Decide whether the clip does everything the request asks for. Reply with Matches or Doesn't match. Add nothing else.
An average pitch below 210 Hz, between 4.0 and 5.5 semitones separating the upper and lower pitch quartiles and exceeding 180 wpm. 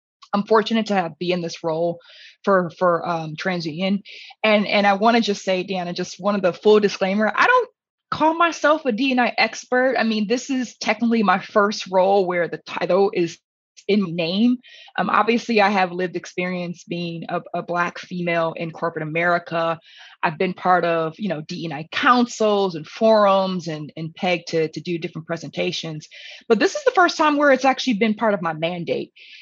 Matches